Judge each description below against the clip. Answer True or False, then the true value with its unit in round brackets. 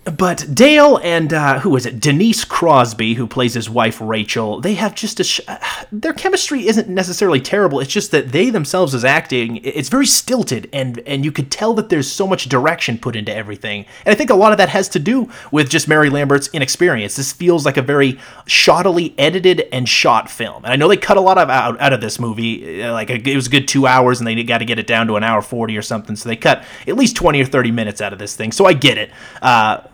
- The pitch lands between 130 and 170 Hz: True (140 Hz)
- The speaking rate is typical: False (245 wpm)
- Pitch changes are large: True (8.0 semitones)